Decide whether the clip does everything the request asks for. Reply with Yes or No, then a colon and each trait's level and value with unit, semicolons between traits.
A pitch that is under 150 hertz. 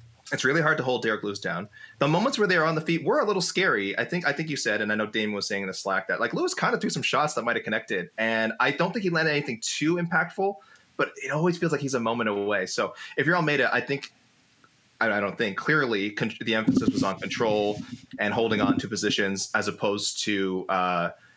Yes: low, 135 Hz